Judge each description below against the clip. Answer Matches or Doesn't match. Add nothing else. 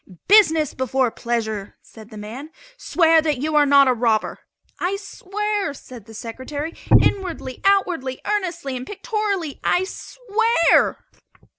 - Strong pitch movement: Matches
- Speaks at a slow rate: Matches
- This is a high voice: Matches